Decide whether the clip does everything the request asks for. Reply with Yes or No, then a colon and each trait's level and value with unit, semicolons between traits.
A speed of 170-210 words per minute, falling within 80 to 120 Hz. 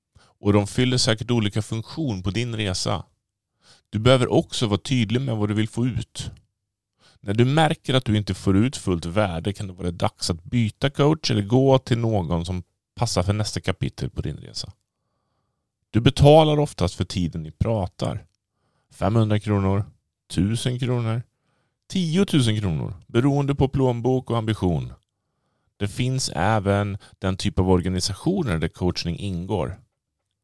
No: average, 155 wpm; low, 110 Hz